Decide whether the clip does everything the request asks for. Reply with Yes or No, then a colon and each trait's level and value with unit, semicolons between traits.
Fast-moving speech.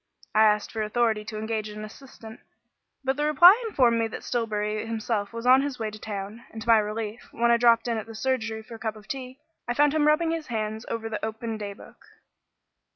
Yes: fast, 225 wpm